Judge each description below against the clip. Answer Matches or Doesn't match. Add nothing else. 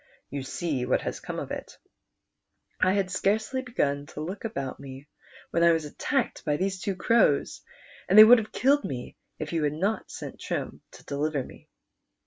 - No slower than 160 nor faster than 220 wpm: Matches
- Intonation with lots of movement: Matches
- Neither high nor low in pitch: Matches